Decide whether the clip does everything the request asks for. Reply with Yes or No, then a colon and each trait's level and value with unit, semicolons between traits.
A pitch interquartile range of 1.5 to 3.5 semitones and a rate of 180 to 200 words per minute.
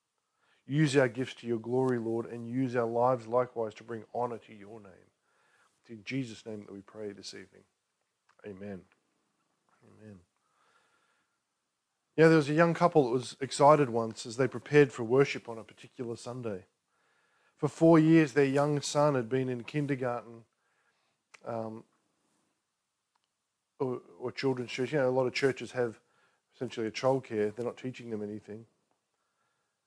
No: average, 3.1 semitones; average, 160 wpm